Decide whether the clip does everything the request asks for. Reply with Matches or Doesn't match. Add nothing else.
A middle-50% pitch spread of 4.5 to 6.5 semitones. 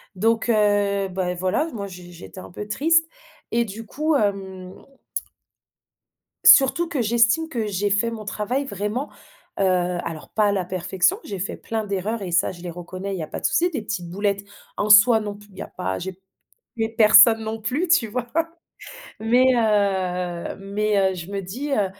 Doesn't match